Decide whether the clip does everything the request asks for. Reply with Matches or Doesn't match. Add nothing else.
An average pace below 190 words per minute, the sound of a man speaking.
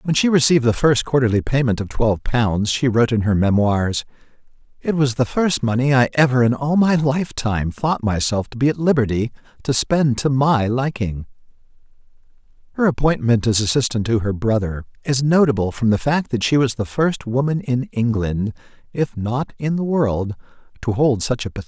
Doesn't match